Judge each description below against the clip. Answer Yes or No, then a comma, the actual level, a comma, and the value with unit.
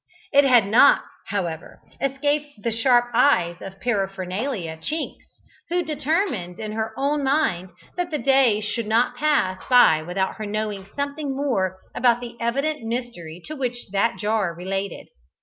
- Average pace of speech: Yes, average, 150 wpm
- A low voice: No, high, 235 Hz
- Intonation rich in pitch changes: Yes, wide, 6.1 semitones